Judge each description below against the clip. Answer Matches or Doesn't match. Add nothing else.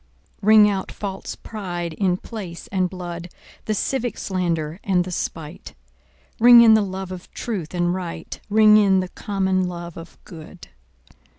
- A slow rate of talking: Doesn't match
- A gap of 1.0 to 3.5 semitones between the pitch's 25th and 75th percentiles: Matches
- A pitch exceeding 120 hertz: Matches